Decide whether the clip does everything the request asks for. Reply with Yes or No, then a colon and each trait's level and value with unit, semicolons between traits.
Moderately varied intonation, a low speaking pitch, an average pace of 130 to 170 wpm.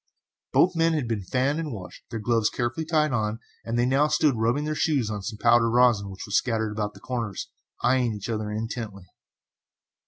No: average, 3.8 semitones; low, 115 Hz; average, 195 wpm